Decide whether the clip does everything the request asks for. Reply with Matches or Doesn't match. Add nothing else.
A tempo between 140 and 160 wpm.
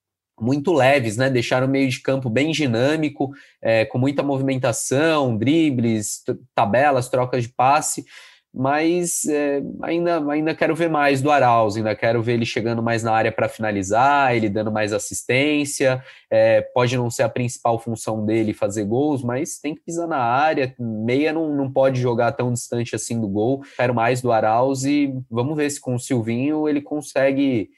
Doesn't match